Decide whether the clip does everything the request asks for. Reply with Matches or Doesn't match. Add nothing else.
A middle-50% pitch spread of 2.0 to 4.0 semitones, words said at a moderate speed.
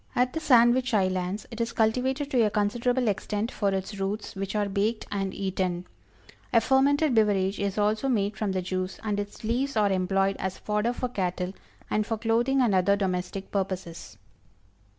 Matches